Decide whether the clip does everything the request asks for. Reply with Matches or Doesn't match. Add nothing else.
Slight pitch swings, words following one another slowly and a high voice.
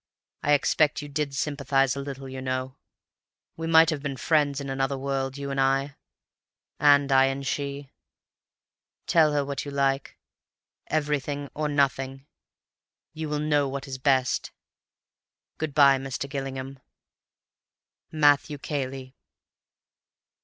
Doesn't match